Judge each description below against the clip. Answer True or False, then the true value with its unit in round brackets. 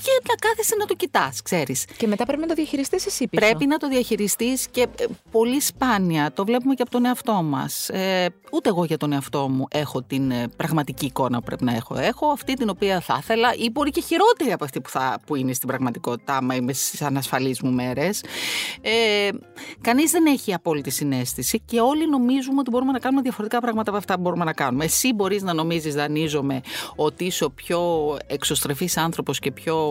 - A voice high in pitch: True (200 Hz)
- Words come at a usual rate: False (195 wpm)